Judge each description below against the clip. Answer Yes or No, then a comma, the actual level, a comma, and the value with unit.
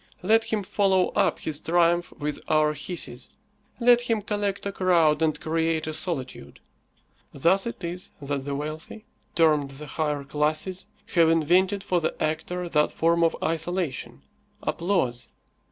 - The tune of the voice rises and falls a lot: No, average, 3.5 semitones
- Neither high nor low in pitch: Yes, medium, 165 Hz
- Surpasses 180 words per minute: No, average, 145 wpm